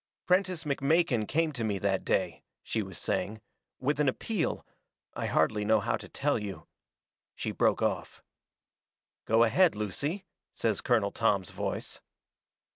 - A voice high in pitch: No, low, 115 Hz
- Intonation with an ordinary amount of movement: No, wide, 6.8 semitones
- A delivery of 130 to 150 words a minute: Yes, average, 140 wpm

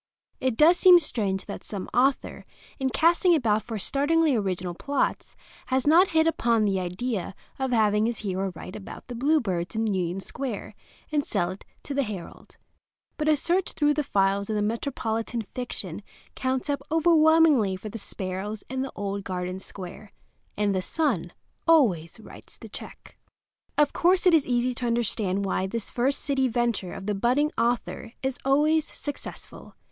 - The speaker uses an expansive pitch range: Yes, wide, 6.4 semitones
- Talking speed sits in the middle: Yes, average, 165 wpm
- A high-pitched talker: Yes, high, 235 Hz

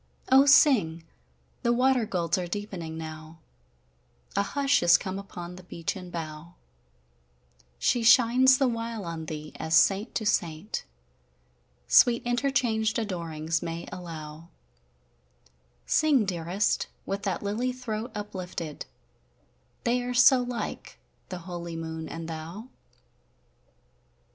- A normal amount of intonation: No, wide, 6.1 semitones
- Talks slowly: Yes, slow, 115 wpm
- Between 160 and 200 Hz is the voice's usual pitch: Yes, high, 190 Hz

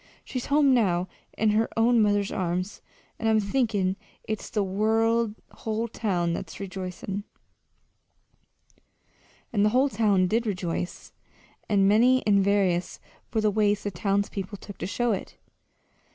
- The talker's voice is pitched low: No, high, 205 Hz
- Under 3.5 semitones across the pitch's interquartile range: Yes, narrow, 2.6 semitones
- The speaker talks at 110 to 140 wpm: Yes, slow, 135 wpm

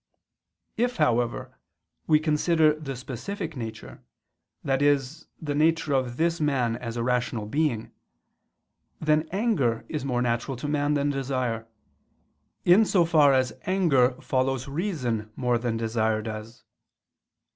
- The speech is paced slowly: Yes, slow, 125 wpm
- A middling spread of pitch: Yes, average, 4.5 semitones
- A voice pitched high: No, low, 135 Hz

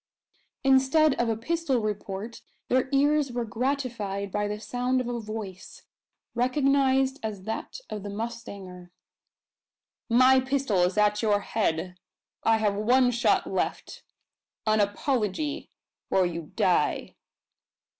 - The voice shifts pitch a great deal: No, average, 4.2 semitones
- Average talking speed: No, slow, 125 wpm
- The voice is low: No, high, 230 Hz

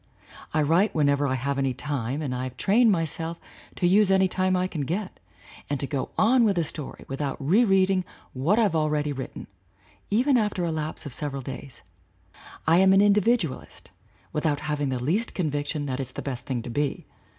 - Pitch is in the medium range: Yes, medium, 155 Hz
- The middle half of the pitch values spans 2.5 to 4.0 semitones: No, wide, 5.5 semitones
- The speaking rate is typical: Yes, average, 195 wpm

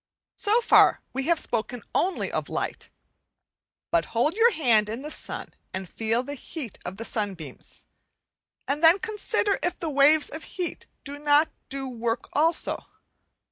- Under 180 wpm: Yes, average, 155 wpm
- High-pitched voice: Yes, very high, 285 Hz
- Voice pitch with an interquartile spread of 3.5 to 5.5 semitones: No, wide, 6.4 semitones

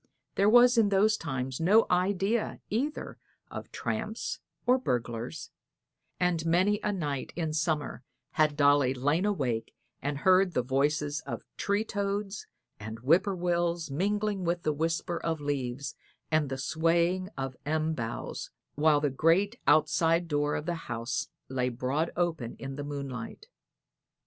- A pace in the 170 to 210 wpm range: No, average, 145 wpm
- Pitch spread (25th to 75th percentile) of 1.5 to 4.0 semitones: No, average, 5.0 semitones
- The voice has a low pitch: No, medium, 160 Hz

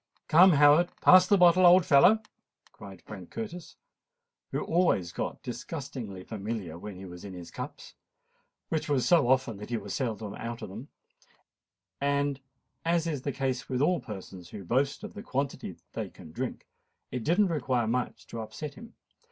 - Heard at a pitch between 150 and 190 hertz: No, low, 130 Hz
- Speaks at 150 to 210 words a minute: Yes, average, 170 wpm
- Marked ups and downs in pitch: Yes, wide, 7.9 semitones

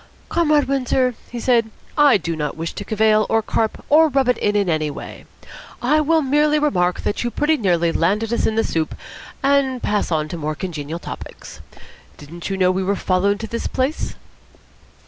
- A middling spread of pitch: No, wide, 7.4 semitones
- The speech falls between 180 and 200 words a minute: Yes, average, 190 wpm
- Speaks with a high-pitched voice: Yes, high, 220 Hz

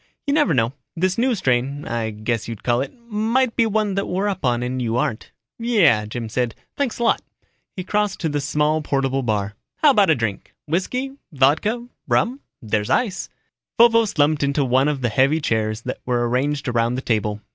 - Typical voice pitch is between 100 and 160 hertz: Yes, medium, 140 Hz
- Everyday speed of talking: Yes, average, 195 wpm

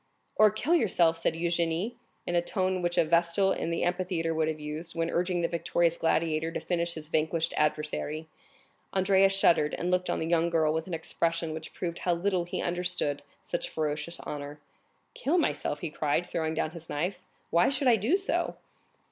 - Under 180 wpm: No, average, 190 wpm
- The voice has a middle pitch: Yes, medium, 170 Hz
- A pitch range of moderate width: No, narrow, 2.1 semitones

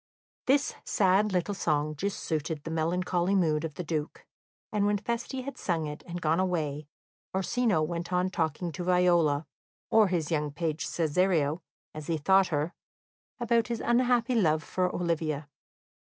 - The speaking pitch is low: No, medium, 175 Hz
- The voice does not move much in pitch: No, average, 3.9 semitones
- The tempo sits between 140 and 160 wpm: Yes, average, 155 wpm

